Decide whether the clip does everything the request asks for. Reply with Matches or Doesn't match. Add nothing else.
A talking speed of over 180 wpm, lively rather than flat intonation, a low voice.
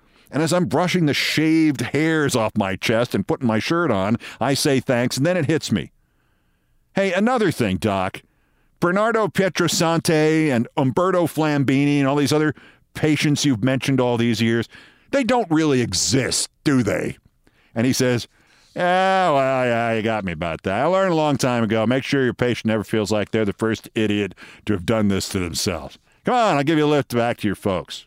Matches